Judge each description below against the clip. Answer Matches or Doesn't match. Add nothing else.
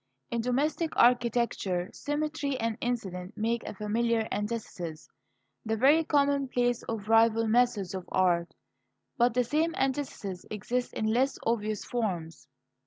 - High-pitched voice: Matches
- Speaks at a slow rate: Matches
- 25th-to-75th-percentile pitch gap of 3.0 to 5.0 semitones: Matches